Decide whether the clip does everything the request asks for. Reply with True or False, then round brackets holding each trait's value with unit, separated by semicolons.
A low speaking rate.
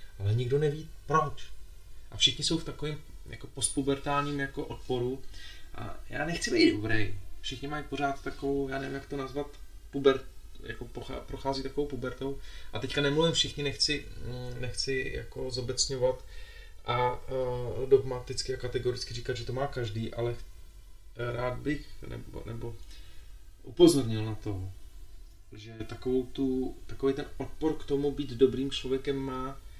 False (140 wpm)